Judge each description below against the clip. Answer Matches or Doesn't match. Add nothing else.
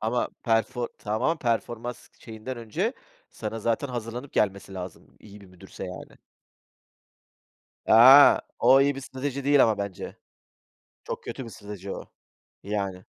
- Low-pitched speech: Matches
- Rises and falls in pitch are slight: Doesn't match